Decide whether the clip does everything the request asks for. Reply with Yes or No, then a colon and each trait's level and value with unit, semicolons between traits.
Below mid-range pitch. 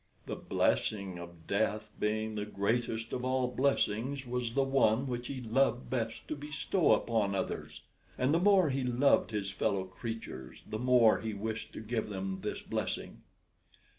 Yes: low, 115 Hz